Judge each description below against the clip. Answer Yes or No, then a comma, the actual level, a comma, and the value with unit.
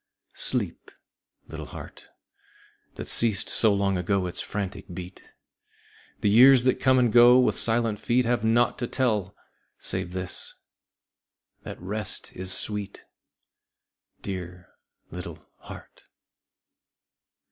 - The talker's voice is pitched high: No, low, 105 Hz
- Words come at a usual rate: No, slow, 115 wpm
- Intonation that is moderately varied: Yes, average, 4.4 semitones